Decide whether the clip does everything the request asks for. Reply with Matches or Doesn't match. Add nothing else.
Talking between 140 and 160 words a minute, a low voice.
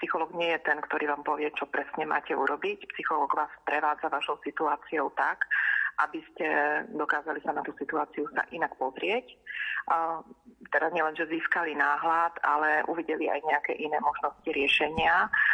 Doesn't match